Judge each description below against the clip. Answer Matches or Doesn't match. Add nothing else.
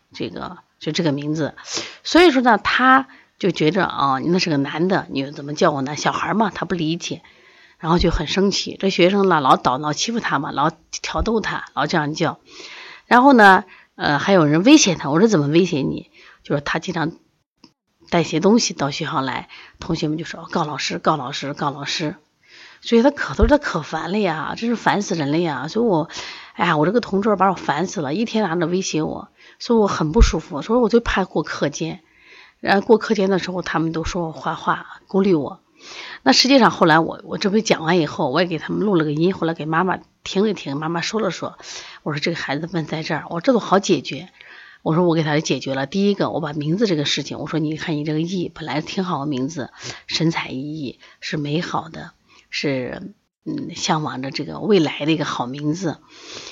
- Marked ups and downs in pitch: Doesn't match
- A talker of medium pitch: Matches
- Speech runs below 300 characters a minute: Doesn't match